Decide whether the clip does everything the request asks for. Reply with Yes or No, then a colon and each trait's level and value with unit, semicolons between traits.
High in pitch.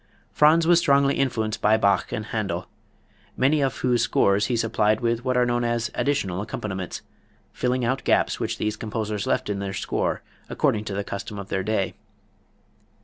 No: low, 110 Hz